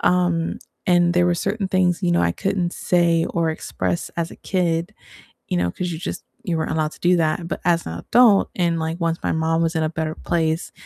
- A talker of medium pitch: Yes, medium, 170 Hz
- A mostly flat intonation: Yes, narrow, 1.8 semitones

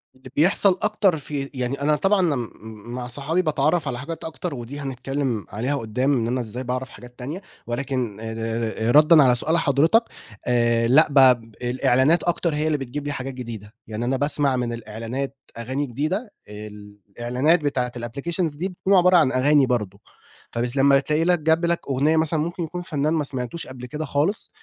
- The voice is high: No, medium, 140 Hz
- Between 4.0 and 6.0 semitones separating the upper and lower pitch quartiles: Yes, average, 4.4 semitones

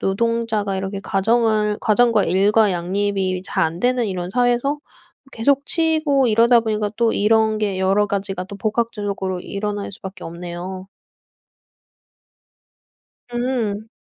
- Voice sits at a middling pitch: No, high, 210 Hz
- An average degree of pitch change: Yes, average, 3.2 semitones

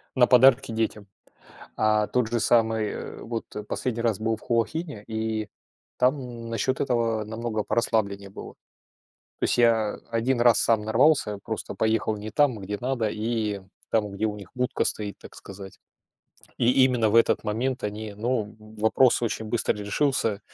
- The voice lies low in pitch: Yes, low, 110 Hz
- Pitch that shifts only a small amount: Yes, narrow, 2.2 semitones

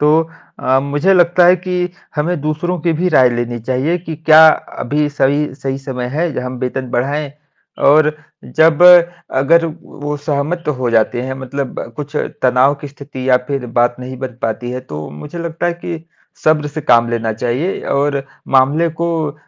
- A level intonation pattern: No, average, 3.8 semitones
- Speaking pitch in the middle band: Yes, medium, 145 Hz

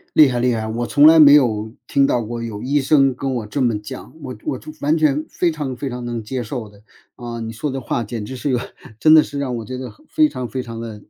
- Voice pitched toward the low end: Yes, low, 125 Hz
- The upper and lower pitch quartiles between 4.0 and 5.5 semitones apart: No, average, 3.6 semitones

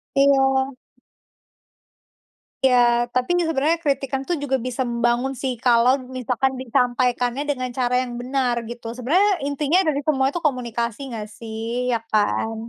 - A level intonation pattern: Yes, narrow, 2.2 semitones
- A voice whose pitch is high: Yes, very high, 255 Hz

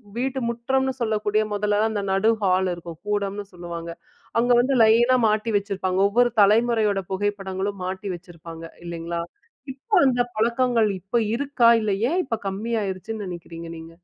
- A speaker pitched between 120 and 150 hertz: No, high, 205 Hz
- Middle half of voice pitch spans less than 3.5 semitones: No, average, 3.9 semitones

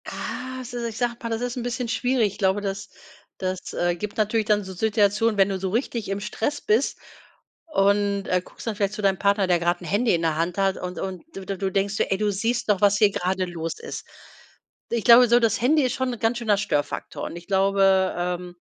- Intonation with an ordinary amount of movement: Yes, average, 3.3 semitones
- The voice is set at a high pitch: Yes, high, 205 Hz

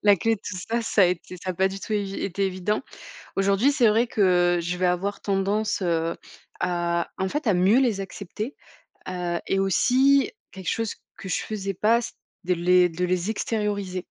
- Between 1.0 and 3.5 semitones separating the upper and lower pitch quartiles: Yes, average, 3.0 semitones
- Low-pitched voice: No, high, 195 Hz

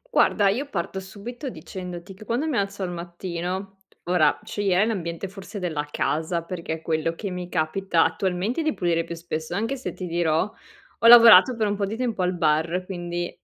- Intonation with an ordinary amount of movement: Yes, average, 3.2 semitones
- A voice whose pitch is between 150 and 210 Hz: Yes, medium, 185 Hz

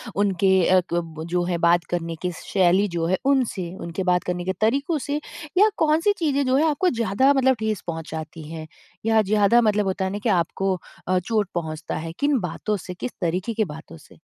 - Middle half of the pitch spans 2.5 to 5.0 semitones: No, wide, 5.4 semitones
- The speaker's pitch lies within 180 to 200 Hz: Yes, high, 190 Hz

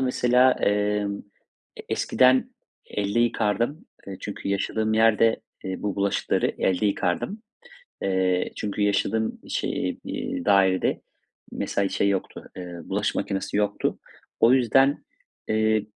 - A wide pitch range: No, narrow, 2.5 semitones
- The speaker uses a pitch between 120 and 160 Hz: No, low, 105 Hz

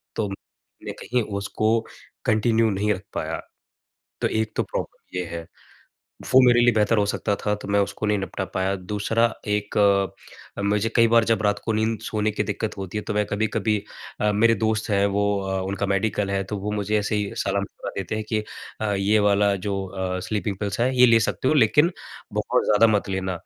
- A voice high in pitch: No, low, 105 Hz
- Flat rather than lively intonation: Yes, narrow, 1.9 semitones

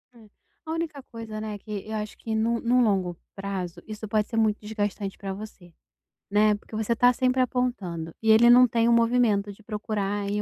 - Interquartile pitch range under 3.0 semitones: Yes, narrow, 2.4 semitones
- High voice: Yes, high, 215 Hz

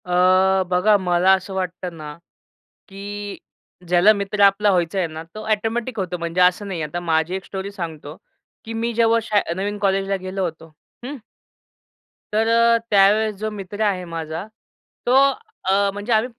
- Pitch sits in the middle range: No, high, 195 Hz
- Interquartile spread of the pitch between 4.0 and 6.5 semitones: No, average, 2.8 semitones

